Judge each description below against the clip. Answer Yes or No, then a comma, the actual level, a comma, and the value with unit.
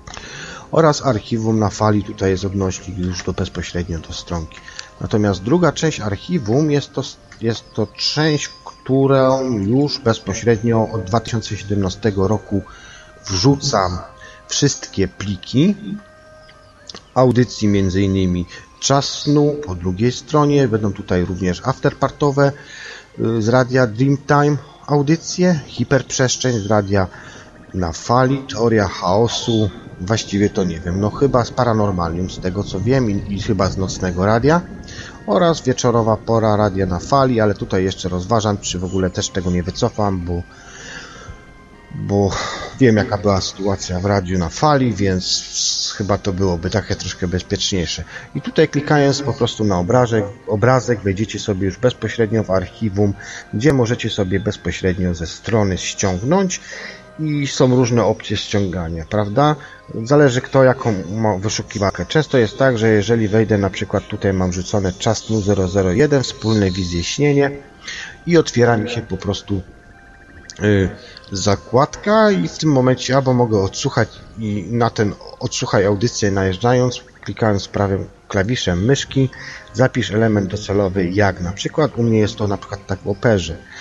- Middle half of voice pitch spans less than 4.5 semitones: No, average, 4.9 semitones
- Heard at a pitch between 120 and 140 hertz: No, low, 105 Hz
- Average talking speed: Yes, average, 135 wpm